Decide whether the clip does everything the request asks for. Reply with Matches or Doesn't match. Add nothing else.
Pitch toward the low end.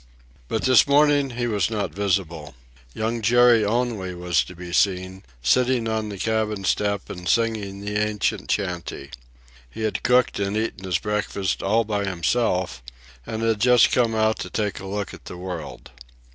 Matches